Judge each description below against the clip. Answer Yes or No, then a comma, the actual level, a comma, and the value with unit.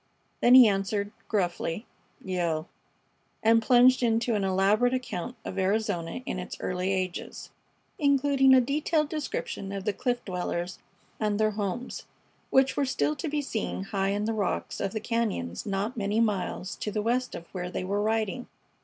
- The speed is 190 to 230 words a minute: No, average, 165 wpm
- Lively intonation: No, average, 4.4 semitones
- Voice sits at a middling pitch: No, high, 210 Hz